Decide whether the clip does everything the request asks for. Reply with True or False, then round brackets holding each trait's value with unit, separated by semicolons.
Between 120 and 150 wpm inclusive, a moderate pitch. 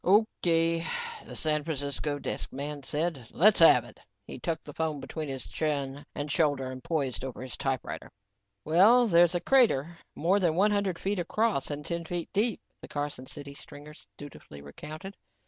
False (165 wpm; 155 Hz)